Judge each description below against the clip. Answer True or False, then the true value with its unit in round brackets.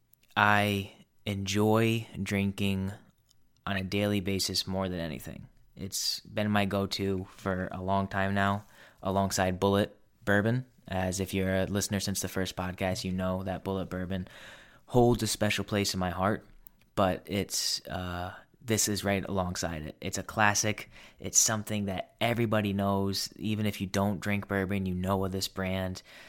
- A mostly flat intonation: True (1.6 semitones)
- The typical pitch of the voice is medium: False (100 Hz)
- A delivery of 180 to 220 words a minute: False (160 wpm)